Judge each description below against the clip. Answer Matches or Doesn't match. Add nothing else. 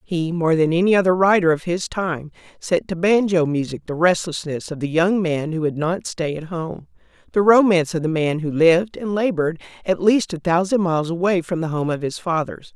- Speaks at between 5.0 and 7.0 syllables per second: Matches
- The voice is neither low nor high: Matches